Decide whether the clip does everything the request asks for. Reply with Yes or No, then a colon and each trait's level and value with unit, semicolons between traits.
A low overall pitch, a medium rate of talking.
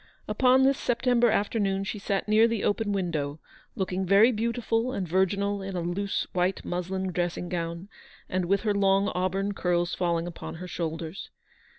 No: high, 195 Hz; average, 165 wpm